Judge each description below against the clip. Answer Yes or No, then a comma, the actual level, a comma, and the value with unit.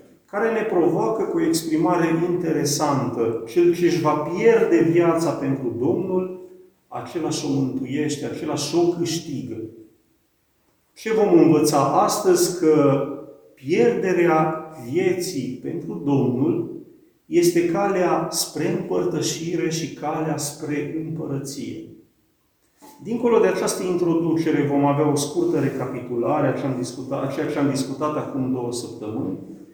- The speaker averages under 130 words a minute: Yes, slow, 115 wpm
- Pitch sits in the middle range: Yes, medium, 155 Hz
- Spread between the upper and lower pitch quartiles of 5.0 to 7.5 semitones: No, average, 4.0 semitones